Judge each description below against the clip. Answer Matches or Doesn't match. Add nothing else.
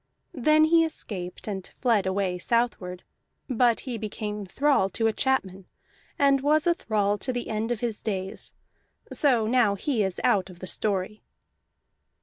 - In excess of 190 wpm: Doesn't match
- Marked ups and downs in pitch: Doesn't match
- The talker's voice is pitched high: Matches